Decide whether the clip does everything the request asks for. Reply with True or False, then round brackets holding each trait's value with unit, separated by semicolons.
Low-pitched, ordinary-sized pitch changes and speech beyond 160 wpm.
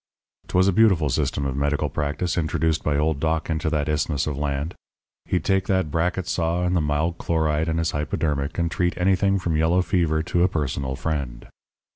True (80 Hz; 3.0 semitones; 190 wpm)